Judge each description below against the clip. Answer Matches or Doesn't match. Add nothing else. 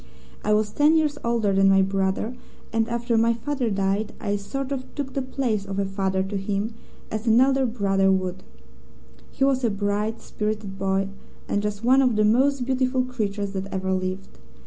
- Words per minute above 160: Matches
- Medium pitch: Doesn't match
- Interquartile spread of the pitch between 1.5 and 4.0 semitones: Doesn't match